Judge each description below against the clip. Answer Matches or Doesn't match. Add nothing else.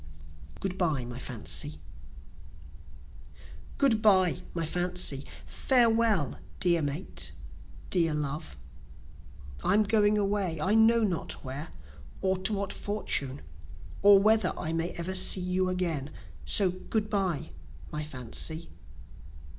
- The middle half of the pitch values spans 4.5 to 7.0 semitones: Matches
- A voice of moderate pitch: Matches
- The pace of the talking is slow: Matches